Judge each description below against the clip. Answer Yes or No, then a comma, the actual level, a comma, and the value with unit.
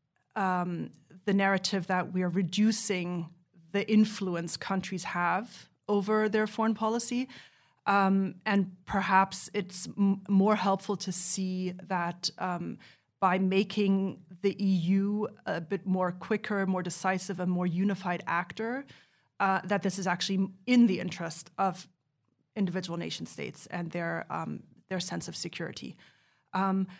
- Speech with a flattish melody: Yes, narrow, 2.0 semitones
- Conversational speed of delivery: Yes, average, 135 wpm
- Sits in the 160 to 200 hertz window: Yes, high, 190 Hz